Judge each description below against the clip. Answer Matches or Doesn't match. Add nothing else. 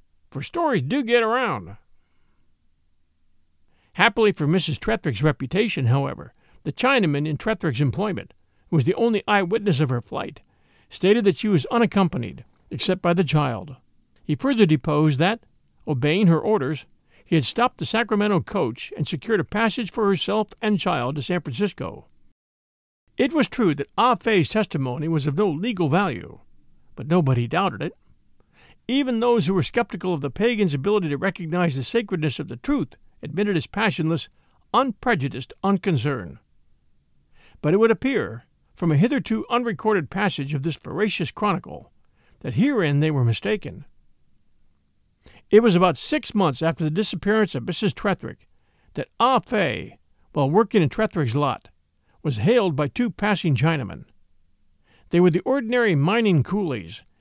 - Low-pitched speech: Doesn't match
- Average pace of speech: Matches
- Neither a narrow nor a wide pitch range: Doesn't match